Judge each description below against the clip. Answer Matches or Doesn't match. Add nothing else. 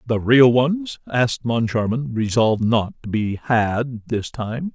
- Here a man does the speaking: Matches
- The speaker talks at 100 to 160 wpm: Matches